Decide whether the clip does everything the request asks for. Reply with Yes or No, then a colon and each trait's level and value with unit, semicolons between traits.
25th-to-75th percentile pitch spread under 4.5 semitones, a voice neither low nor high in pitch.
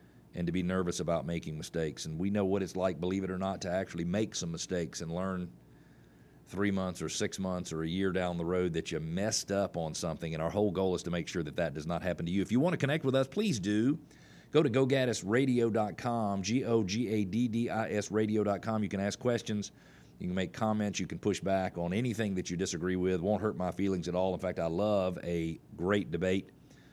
No: average, 3.4 semitones; very low, 95 Hz